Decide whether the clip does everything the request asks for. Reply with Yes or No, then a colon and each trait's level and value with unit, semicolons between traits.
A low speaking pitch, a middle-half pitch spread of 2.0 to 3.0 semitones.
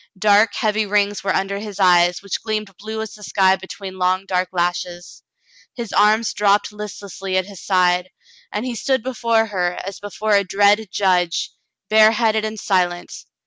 No: high, 200 Hz; narrow, 2.4 semitones